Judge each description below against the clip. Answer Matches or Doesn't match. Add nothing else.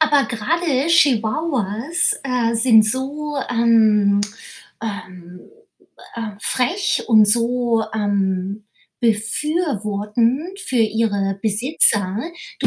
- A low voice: Doesn't match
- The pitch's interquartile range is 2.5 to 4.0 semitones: Doesn't match